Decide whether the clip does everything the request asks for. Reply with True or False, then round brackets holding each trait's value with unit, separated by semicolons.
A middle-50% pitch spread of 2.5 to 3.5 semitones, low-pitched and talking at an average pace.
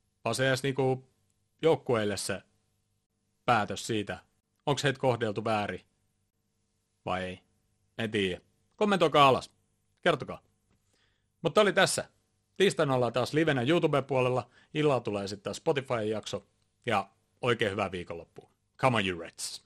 False (4.2 semitones; 110 Hz; 115 wpm)